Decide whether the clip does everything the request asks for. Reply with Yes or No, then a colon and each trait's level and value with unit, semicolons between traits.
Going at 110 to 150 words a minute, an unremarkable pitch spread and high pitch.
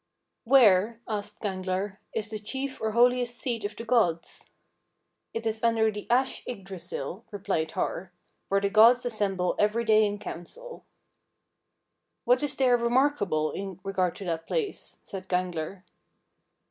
Yes: average, 145 wpm; average, 4.1 semitones; high, 215 Hz